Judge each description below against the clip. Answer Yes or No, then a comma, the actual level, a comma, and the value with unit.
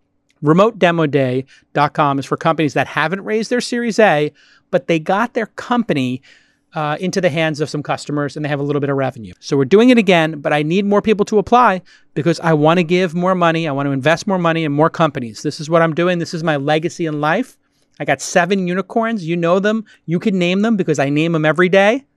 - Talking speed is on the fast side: Yes, fast, 235 wpm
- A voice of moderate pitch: Yes, medium, 165 Hz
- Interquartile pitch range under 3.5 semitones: No, average, 4.6 semitones